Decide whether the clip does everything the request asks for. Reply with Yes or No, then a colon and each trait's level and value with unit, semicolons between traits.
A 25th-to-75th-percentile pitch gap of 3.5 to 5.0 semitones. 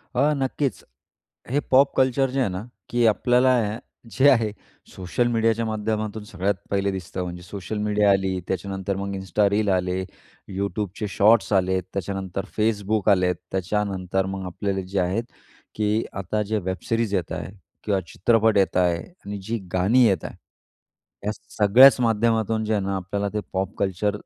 No: average, 2.8 semitones